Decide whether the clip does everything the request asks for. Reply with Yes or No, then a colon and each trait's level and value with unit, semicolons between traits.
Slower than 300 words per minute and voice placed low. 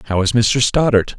Yes: average, 200 wpm; low, 115 Hz